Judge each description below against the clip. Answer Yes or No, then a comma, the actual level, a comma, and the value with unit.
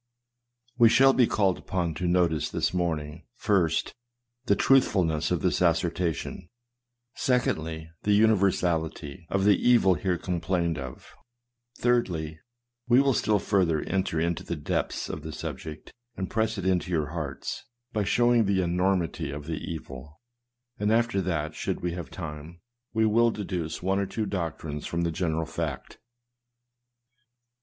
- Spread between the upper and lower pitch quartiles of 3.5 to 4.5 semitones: Yes, average, 3.9 semitones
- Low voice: Yes, very low, 90 Hz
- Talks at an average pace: Yes, average, 150 wpm